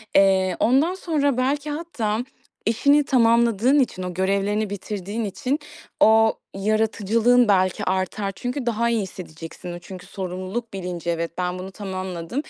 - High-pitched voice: Yes, high, 210 Hz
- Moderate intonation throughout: Yes, average, 4.3 semitones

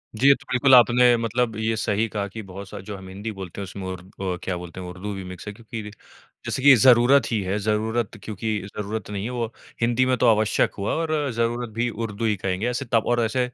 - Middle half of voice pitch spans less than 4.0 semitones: Yes, average, 3.4 semitones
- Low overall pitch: Yes, low, 110 Hz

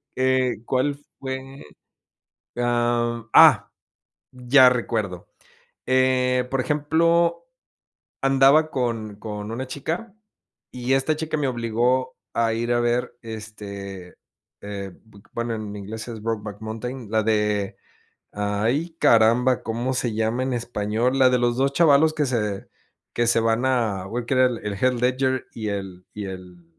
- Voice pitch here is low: Yes, low, 120 Hz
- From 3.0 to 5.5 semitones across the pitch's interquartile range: Yes, average, 3.3 semitones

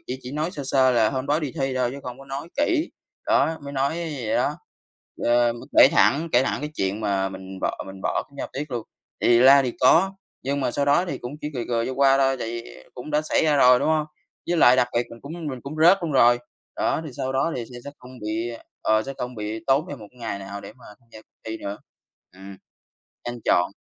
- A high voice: No, low, 130 Hz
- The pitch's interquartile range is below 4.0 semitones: Yes, average, 3.5 semitones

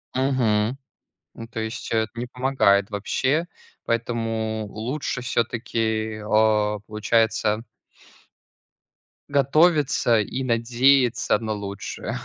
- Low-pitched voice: Yes, low, 115 Hz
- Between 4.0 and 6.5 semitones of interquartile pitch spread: No, average, 2.9 semitones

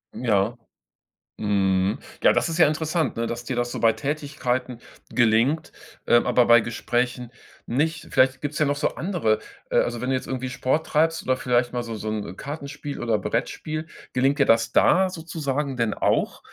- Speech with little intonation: No, average, 4.1 semitones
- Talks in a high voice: No, low, 130 Hz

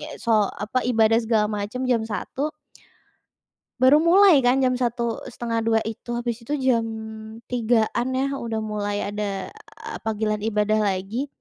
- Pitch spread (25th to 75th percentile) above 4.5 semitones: No, average, 2.8 semitones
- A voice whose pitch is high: Yes, high, 230 Hz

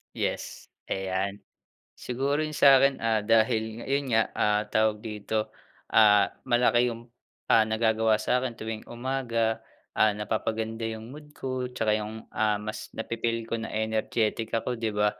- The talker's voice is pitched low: Yes, low, 110 Hz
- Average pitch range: No, narrow, 1.8 semitones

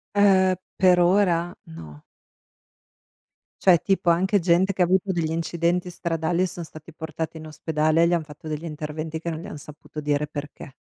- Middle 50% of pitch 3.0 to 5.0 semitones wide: No, narrow, 2.5 semitones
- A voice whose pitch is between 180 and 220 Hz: No, medium, 165 Hz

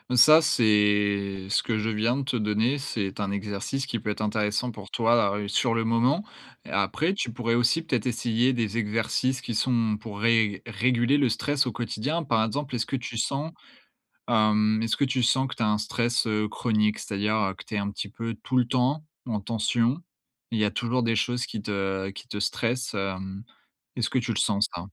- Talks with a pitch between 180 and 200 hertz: No, low, 115 Hz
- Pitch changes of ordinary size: Yes, average, 3.0 semitones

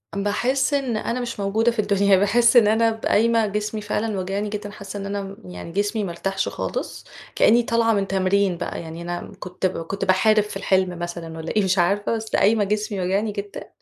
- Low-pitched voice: No, high, 205 Hz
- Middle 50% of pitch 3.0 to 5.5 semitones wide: No, narrow, 2.5 semitones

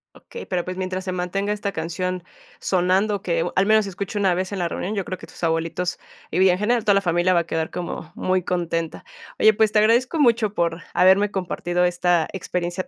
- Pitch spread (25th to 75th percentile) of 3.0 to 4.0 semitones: No, narrow, 2.5 semitones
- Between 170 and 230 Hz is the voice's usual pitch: Yes, medium, 185 Hz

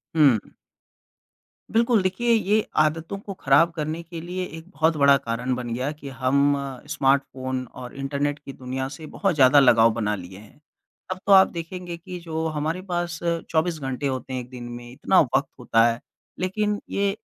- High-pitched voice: No, medium, 150 Hz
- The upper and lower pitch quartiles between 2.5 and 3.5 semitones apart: No, average, 5.1 semitones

